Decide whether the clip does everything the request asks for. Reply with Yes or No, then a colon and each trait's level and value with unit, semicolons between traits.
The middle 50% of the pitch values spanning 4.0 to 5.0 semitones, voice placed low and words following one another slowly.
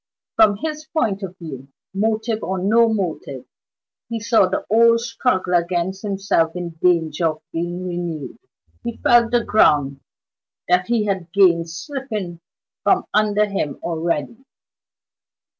No: average, 4.6 semitones; high, 190 Hz; slow, 130 wpm